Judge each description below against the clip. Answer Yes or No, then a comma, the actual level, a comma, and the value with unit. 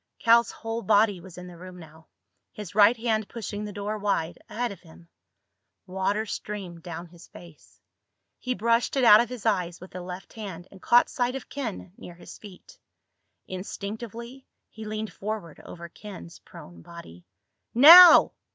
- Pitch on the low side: No, high, 205 Hz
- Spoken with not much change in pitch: No, average, 4.2 semitones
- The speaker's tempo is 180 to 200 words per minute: No, average, 165 wpm